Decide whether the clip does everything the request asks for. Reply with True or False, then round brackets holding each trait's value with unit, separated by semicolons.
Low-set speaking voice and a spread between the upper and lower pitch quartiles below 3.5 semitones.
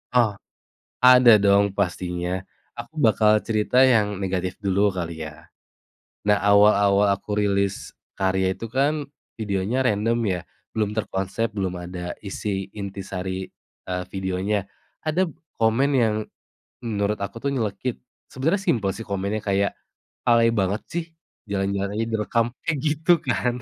True (105 Hz; 3.1 semitones)